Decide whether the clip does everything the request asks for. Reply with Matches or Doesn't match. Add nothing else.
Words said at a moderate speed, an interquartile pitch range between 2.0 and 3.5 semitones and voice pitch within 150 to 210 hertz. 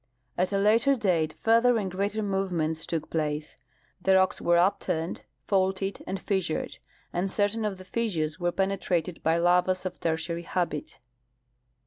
Matches